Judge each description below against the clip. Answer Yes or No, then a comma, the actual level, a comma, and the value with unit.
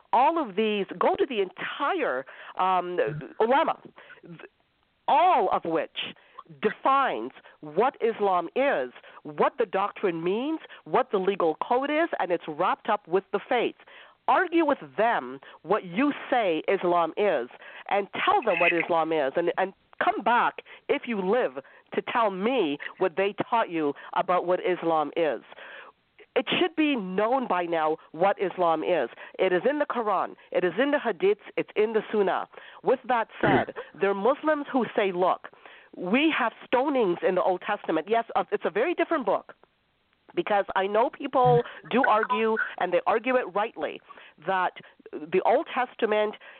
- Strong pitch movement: Yes, wide, 7.0 semitones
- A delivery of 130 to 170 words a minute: Yes, average, 160 wpm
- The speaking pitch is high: Yes, high, 215 Hz